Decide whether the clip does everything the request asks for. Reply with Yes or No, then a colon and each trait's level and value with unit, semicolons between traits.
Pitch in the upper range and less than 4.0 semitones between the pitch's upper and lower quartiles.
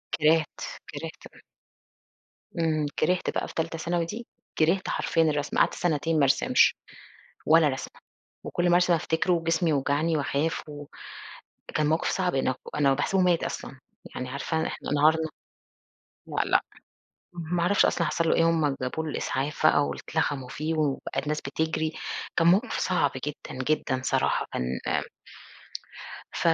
No: medium, 160 Hz; narrow, 2.4 semitones